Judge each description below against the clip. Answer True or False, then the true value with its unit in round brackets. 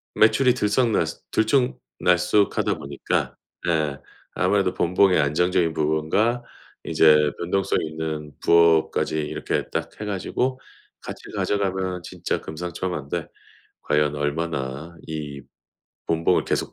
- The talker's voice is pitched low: True (85 Hz)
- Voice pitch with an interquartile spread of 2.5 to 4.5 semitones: True (4.1 semitones)